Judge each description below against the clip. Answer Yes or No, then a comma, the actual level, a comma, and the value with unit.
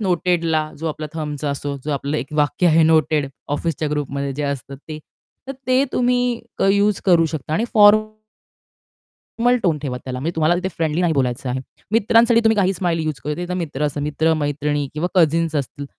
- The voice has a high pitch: No, medium, 155 Hz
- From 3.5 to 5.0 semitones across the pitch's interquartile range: Yes, average, 3.8 semitones